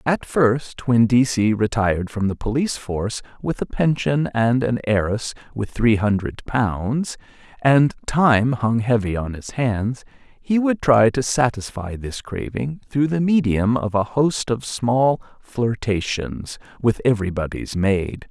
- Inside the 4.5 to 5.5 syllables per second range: No, 4.0 syllables/s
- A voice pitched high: No, low, 120 Hz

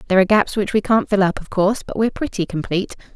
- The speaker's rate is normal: No, fast, 265 wpm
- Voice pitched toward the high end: Yes, high, 200 Hz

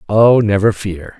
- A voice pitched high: No, low, 105 Hz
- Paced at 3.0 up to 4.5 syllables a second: Yes, 4.0 syllables/s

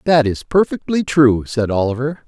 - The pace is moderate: Yes, average, 160 wpm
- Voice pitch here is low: Yes, low, 130 Hz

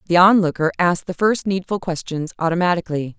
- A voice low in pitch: No, medium, 175 Hz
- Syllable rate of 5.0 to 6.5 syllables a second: Yes, 6.3 syllables/s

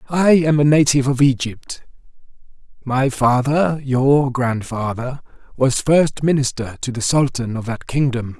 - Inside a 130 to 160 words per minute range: Yes, slow, 135 wpm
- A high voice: No, low, 135 Hz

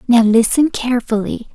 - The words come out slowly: Yes, slow, 115 wpm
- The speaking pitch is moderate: No, high, 240 Hz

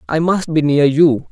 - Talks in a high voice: No, medium, 155 Hz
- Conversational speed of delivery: No, fast, 230 wpm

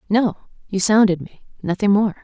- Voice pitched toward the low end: No, high, 200 Hz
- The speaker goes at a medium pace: Yes, average, 160 wpm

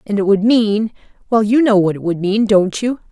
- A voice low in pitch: No, high, 210 Hz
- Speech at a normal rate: No, fast, 230 wpm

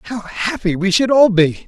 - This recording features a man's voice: Yes, male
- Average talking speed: No, fast, 215 wpm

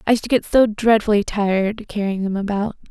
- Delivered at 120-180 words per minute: No, fast, 205 wpm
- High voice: Yes, high, 210 Hz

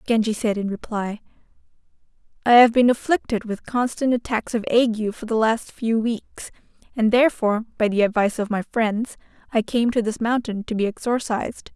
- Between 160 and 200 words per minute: Yes, average, 175 wpm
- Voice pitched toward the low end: No, high, 225 Hz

